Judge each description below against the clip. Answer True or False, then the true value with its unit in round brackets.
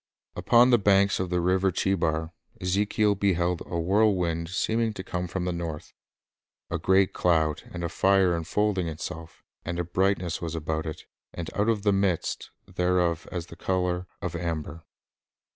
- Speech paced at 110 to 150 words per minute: False (160 wpm)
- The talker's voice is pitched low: True (90 Hz)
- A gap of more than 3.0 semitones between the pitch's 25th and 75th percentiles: False (2.5 semitones)